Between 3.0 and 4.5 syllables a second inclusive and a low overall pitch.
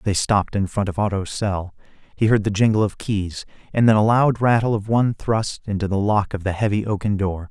No: 5.5 syllables/s; low, 105 Hz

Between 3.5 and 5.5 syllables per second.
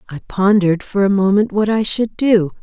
Yes: 5.2 syllables/s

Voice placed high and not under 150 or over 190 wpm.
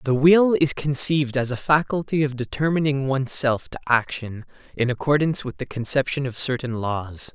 No: low, 135 Hz; average, 165 wpm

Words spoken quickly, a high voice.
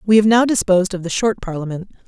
Yes: fast, 230 wpm; high, 195 Hz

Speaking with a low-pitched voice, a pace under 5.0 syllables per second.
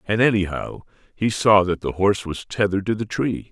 No: low, 100 Hz; 5.5 syllables/s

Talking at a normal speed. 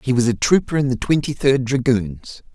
No: fast, 235 wpm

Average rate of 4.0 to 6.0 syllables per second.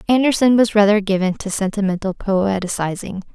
Yes: 5.2 syllables/s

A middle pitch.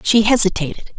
No: high, 205 Hz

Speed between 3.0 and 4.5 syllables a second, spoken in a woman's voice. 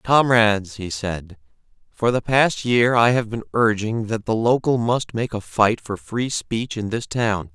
No: 4.1 syllables/s; male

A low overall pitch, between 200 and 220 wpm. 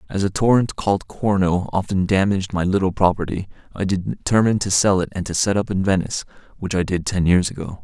Yes: very low, 95 Hz; fast, 205 wpm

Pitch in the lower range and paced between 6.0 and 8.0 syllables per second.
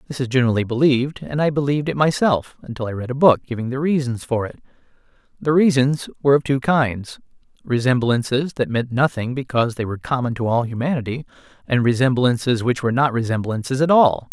Yes: low, 130 Hz; 6.2 syllables/s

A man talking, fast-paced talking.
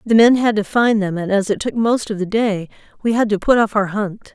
No: female; fast, 290 wpm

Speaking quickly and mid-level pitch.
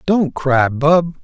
No: average, 145 wpm; medium, 150 Hz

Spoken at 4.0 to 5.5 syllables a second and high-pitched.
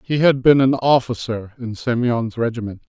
No: 4.9 syllables/s; low, 120 Hz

